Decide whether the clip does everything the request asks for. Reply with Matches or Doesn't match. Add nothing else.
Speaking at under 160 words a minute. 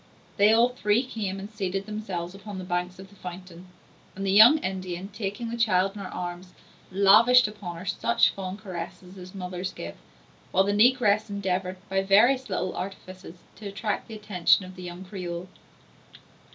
Doesn't match